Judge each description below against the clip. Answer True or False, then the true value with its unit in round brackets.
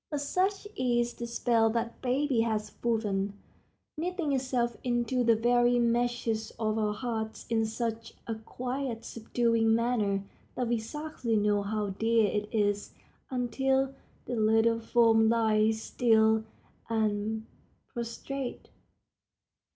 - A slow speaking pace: True (120 wpm)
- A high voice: True (230 Hz)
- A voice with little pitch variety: True (1.9 semitones)